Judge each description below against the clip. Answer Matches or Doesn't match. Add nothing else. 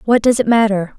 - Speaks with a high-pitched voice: Matches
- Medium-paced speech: Doesn't match